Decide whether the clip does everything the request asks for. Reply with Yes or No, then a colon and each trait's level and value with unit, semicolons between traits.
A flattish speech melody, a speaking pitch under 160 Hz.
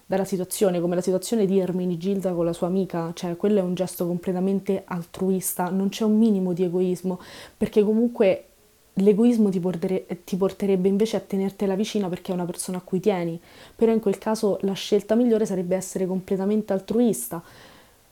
No: narrow, 2.1 semitones; high, 190 Hz